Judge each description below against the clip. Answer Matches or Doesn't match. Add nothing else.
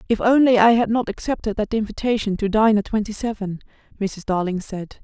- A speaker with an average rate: Matches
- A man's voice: Doesn't match